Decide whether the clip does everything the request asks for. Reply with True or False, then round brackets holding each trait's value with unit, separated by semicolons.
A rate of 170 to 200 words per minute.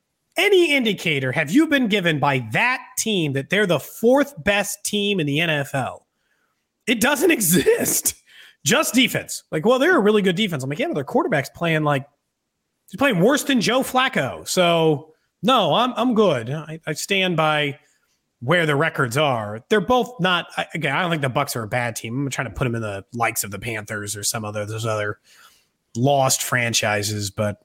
True (195 wpm)